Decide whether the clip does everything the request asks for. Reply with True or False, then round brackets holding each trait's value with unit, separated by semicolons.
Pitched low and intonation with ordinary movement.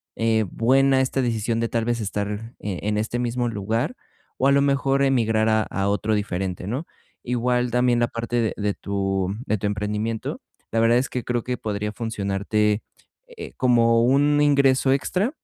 True (115 Hz; 3.1 semitones)